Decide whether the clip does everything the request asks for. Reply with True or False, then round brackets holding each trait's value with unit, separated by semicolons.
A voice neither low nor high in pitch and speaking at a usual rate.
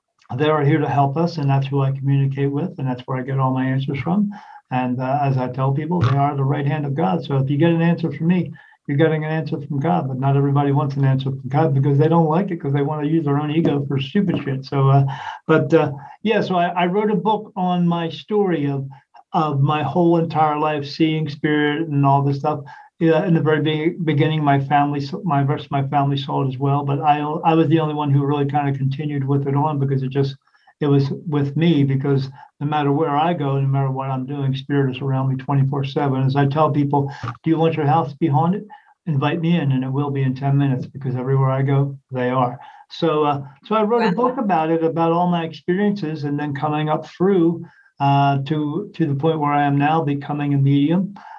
False (145 Hz; 245 wpm)